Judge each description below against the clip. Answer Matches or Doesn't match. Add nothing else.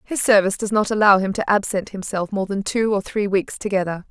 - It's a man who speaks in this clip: Doesn't match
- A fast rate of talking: Matches